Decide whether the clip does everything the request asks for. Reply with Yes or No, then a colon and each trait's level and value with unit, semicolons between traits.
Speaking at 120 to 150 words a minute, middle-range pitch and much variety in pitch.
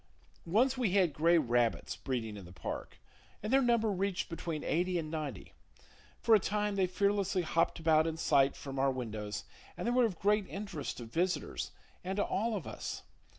No: average, 190 wpm; medium, 175 Hz; wide, 6.6 semitones